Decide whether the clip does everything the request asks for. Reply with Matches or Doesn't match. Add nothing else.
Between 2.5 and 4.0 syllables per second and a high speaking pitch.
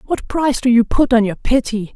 Doesn't match